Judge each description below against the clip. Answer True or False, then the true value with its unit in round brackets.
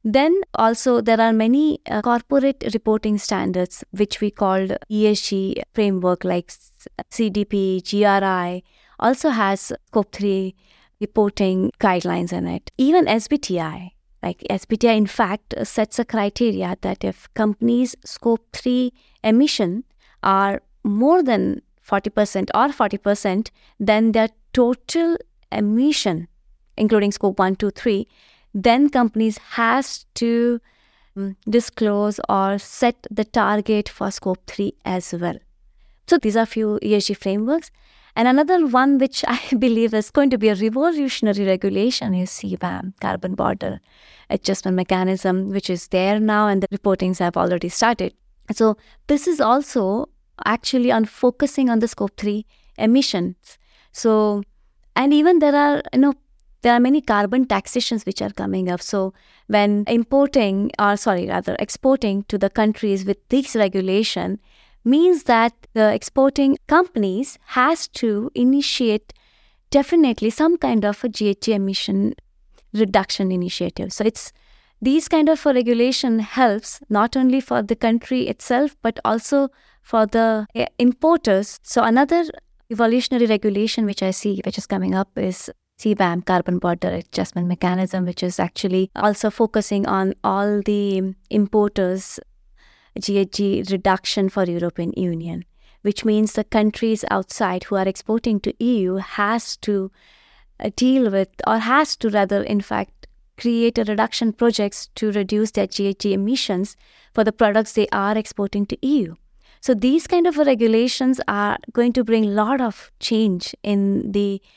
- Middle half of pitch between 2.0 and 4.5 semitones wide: True (3.8 semitones)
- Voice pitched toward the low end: False (215 Hz)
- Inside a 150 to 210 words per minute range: False (140 wpm)